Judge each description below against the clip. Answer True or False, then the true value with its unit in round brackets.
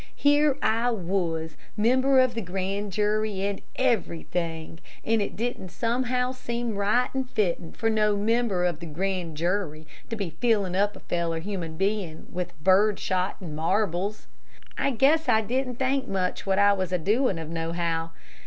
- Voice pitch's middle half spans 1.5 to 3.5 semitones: False (4.9 semitones)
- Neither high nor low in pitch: False (200 Hz)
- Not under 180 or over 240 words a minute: False (170 wpm)